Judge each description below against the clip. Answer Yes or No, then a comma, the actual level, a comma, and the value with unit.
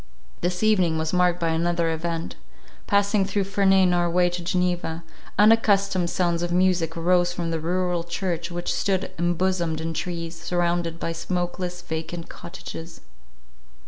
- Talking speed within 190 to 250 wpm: No, average, 145 wpm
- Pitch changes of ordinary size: No, narrow, 1.6 semitones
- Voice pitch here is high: No, medium, 175 Hz